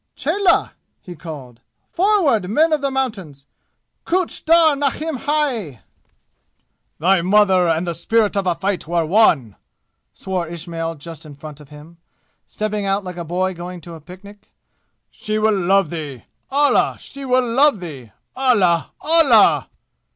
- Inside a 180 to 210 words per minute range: No, average, 145 wpm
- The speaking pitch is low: No, high, 190 Hz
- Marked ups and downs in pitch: Yes, wide, 7.3 semitones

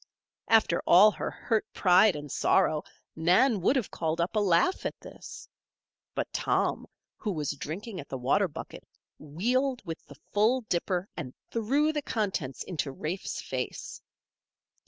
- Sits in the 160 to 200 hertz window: Yes, medium, 185 Hz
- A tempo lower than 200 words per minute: Yes, average, 150 wpm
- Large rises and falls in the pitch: Yes, wide, 5.8 semitones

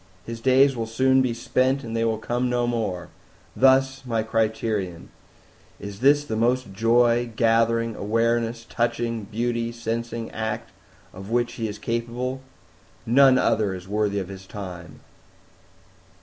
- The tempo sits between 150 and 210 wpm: No, average, 140 wpm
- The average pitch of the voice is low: Yes, low, 115 Hz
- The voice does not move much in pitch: Yes, narrow, 1.8 semitones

